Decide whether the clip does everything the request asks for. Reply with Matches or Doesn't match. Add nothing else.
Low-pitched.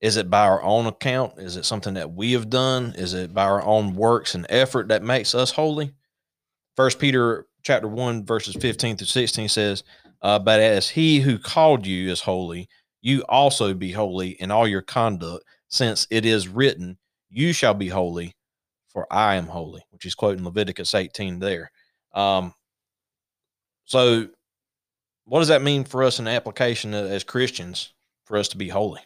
Matches